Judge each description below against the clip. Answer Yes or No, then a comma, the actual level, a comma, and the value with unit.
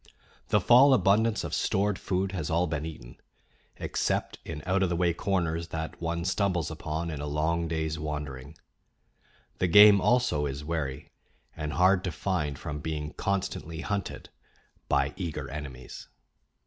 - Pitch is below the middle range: Yes, very low, 85 Hz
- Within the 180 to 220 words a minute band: No, average, 150 wpm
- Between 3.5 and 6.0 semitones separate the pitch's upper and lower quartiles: Yes, average, 3.8 semitones